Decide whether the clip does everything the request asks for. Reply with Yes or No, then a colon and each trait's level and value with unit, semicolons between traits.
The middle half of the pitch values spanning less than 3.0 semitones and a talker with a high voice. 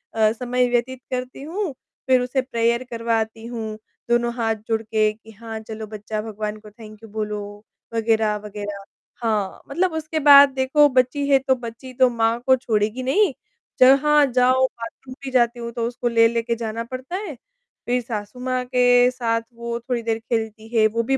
Yes: narrow, 2.6 semitones; high, 235 Hz